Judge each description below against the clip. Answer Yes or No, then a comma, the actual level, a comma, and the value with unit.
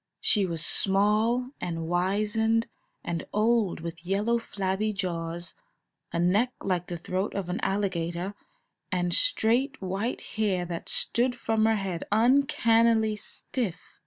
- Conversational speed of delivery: No, slow, 130 wpm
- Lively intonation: No, average, 4.1 semitones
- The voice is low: No, high, 200 Hz